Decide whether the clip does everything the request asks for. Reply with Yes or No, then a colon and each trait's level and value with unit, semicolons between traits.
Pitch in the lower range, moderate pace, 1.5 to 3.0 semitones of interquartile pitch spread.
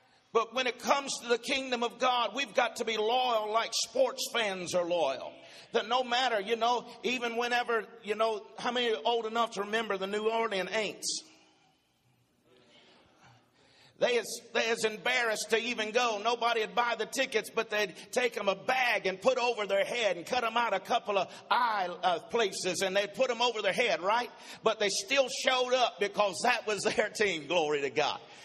No: high, 230 Hz; average, 195 wpm; average, 2.7 semitones